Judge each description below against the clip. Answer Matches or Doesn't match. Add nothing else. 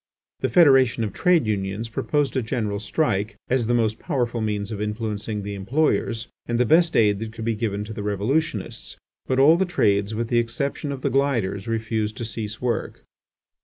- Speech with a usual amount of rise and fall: Matches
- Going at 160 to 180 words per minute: Doesn't match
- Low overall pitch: Matches